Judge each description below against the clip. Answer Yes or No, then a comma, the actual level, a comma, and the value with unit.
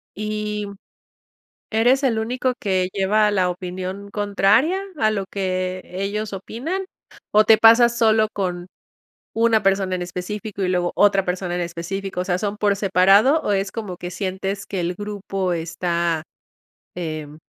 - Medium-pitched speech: No, high, 195 Hz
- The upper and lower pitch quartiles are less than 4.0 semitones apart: Yes, average, 2.8 semitones